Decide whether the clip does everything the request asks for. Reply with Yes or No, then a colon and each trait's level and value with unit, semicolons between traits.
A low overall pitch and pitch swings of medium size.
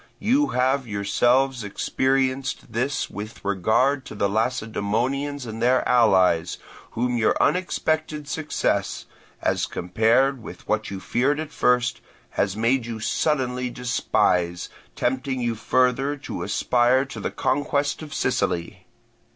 Yes: low, 125 Hz; average, 3.7 semitones